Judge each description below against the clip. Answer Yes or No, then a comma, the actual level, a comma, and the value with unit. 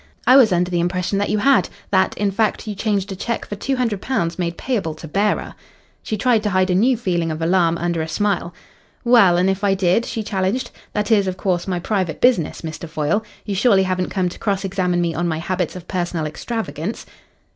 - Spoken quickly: Yes, fast, 215 wpm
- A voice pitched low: No, high, 190 Hz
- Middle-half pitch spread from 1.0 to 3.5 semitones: Yes, average, 3.2 semitones